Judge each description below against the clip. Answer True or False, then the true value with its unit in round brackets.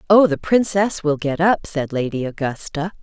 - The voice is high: False (165 Hz)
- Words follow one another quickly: False (180 wpm)